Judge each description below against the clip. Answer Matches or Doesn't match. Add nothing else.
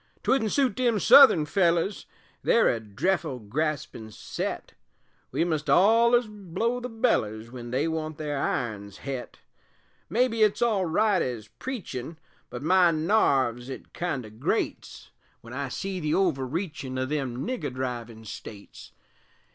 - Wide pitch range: Matches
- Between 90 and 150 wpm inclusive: Matches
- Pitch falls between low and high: Matches